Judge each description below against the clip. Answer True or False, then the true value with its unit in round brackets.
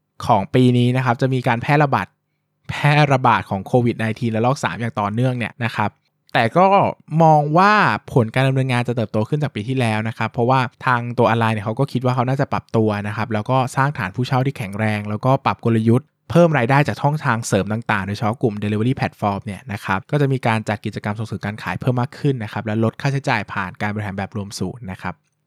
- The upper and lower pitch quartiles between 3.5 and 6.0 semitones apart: True (4.0 semitones)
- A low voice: True (120 Hz)